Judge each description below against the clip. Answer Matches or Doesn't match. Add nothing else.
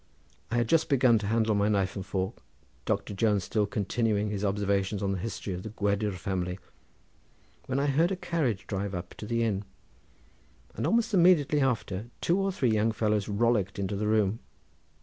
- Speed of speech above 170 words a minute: Matches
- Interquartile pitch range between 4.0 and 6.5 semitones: Doesn't match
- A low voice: Matches